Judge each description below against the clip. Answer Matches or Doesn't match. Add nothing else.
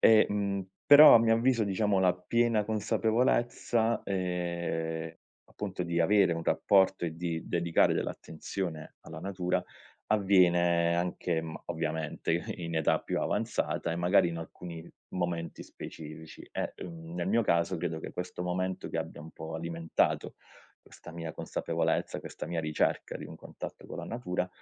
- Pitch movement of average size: Matches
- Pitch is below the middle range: Matches